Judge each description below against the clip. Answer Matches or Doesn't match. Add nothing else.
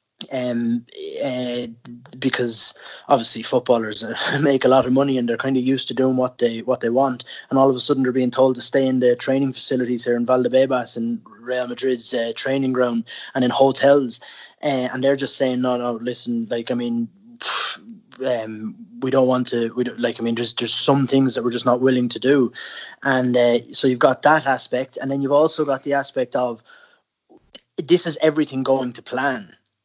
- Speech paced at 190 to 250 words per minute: Matches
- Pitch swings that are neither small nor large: Doesn't match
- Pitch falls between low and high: Doesn't match